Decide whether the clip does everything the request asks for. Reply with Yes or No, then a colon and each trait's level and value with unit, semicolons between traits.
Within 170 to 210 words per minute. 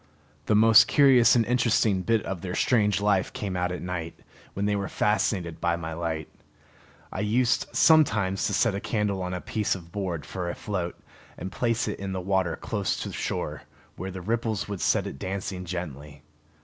Yes: average, 190 wpm